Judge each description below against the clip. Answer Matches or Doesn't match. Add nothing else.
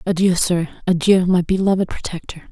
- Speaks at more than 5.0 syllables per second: Matches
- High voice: Doesn't match